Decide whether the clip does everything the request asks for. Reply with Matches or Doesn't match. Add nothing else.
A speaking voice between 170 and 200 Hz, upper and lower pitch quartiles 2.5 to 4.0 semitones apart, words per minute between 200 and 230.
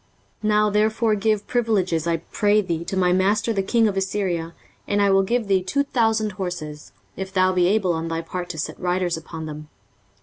Matches